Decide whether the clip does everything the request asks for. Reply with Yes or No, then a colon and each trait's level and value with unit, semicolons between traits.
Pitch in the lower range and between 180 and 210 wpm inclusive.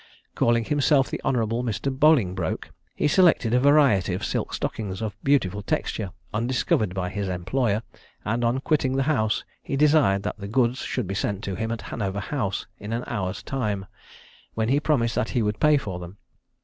Yes: low, 115 Hz; average, 185 wpm